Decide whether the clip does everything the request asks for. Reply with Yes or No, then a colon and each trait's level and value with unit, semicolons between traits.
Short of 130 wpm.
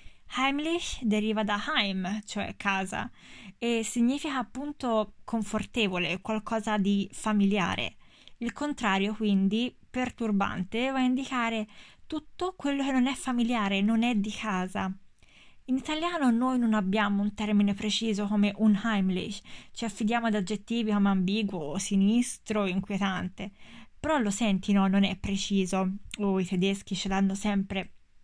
No: average, 135 wpm